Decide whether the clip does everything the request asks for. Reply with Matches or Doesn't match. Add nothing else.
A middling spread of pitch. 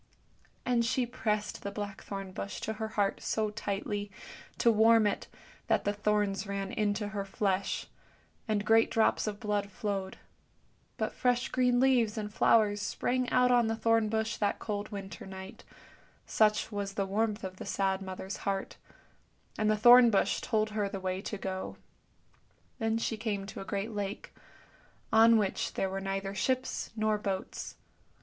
Doesn't match